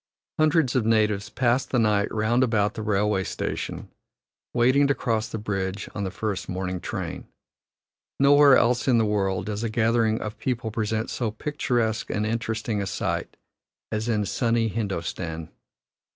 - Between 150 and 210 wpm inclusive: Yes, average, 155 wpm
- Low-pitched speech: Yes, low, 110 Hz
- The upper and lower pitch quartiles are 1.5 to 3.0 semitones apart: Yes, narrow, 2.4 semitones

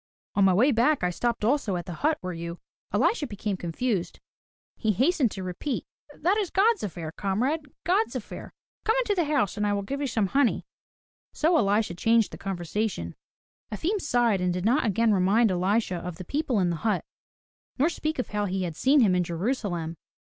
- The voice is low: No, high, 215 Hz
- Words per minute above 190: Yes, average, 200 wpm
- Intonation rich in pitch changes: Yes, wide, 7.4 semitones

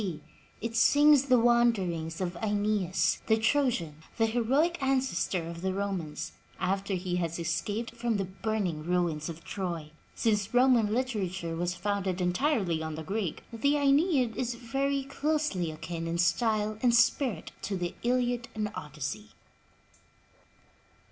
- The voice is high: Yes, high, 205 Hz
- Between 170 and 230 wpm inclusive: No, average, 140 wpm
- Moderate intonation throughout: No, wide, 5.7 semitones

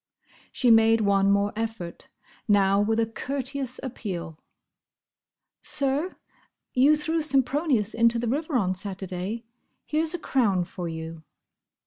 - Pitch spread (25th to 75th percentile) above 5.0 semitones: Yes, wide, 5.5 semitones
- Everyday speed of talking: No, slow, 110 wpm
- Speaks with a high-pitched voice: Yes, high, 225 Hz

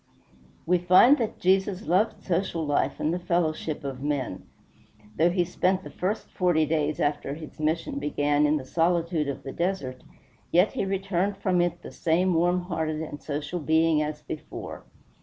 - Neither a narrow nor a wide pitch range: Yes, average, 3.2 semitones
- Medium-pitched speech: Yes, medium, 165 Hz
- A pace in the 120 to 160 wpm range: No, average, 170 wpm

